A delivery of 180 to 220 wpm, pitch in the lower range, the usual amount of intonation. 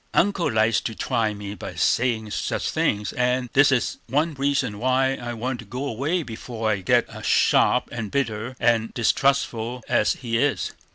No: average, 170 wpm; low, 120 Hz; average, 3.3 semitones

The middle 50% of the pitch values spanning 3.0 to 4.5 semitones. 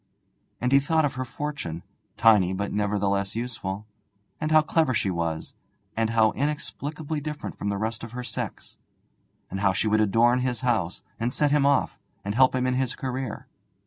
No: average, 5.2 semitones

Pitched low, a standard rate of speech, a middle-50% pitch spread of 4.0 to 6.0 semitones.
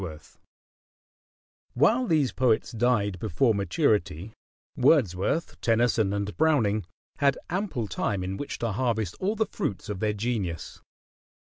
No: low, 110 Hz; slow, 125 wpm; wide, 5.5 semitones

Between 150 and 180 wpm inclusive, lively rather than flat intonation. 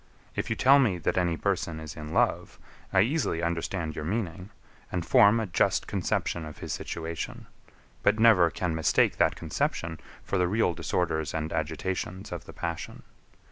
No: average, 170 wpm; average, 3.4 semitones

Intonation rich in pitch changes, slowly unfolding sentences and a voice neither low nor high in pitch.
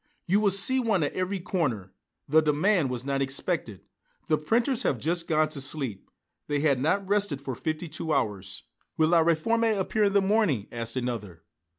No: wide, 6.6 semitones; average, 185 wpm; medium, 155 Hz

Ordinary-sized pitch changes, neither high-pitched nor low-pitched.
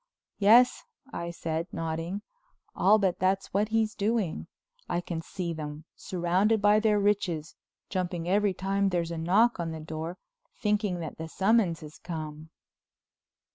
Yes: average, 4.0 semitones; medium, 180 Hz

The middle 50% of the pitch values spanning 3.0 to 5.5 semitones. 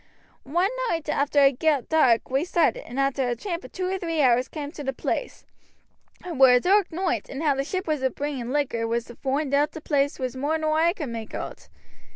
Yes: average, 3.7 semitones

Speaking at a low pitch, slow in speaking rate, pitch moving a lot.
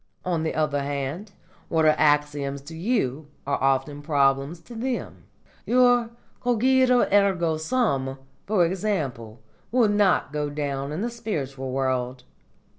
No: medium, 155 Hz; slow, 130 wpm; wide, 7.2 semitones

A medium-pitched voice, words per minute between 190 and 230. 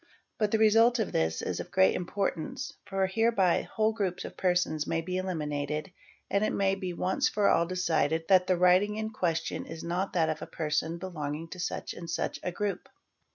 Yes: medium, 180 Hz; average, 200 wpm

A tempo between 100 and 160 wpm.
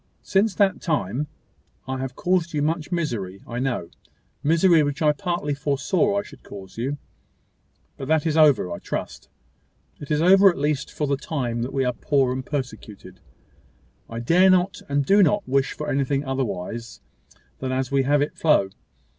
No: average, 175 wpm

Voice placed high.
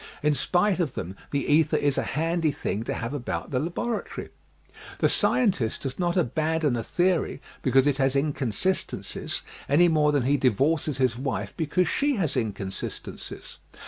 No: medium, 145 Hz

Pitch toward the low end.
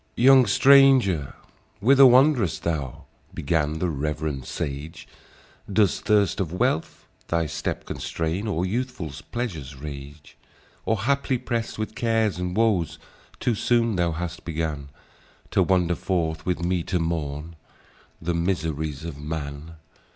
Yes: very low, 85 Hz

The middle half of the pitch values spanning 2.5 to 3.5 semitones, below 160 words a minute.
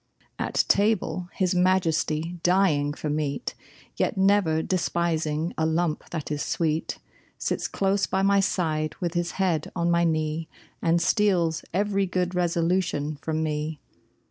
Yes: average, 2.9 semitones; average, 140 wpm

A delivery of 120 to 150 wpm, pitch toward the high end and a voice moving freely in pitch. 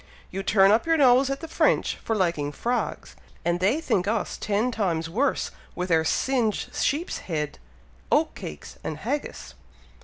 No: average, 160 wpm; high, 205 Hz; wide, 6.9 semitones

